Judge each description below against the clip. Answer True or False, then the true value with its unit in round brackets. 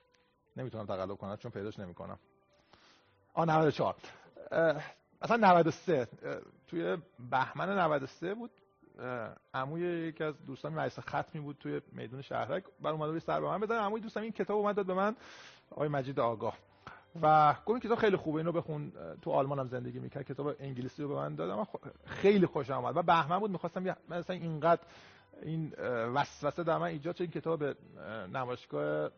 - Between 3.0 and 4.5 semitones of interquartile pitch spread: False (5.2 semitones)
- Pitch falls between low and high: True (155 Hz)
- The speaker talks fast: True (170 wpm)